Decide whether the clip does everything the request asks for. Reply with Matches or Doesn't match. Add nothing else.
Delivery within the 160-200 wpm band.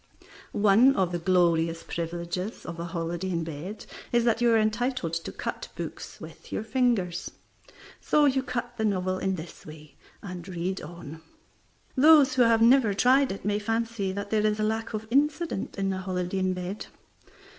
Matches